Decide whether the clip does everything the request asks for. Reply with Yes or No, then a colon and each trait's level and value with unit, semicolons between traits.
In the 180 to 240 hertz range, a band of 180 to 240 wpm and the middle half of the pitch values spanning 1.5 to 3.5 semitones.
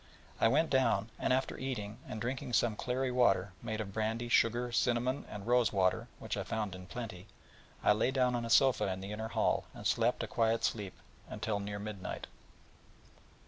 No: low, 110 Hz; average, 185 wpm; average, 3.1 semitones